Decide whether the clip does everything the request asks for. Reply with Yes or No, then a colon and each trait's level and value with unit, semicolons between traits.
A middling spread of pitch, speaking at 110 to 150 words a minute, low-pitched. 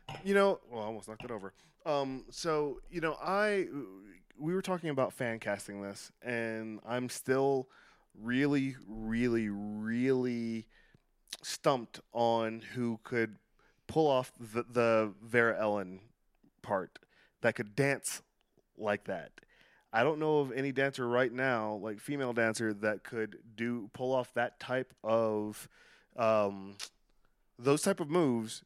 Yes: average, 3.5 semitones; average, 140 wpm; low, 120 Hz